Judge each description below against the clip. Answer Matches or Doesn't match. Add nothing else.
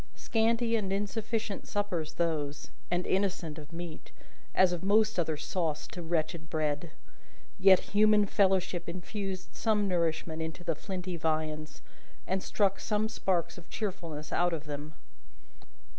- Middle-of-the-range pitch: Matches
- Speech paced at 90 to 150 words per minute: Matches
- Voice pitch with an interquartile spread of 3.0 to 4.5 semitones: Matches